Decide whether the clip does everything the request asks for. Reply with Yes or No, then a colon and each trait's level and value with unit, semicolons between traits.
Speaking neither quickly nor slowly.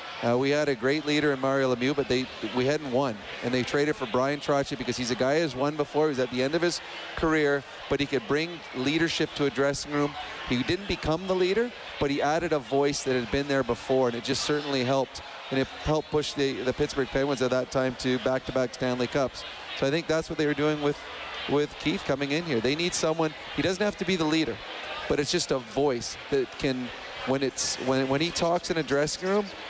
No: fast, 240 wpm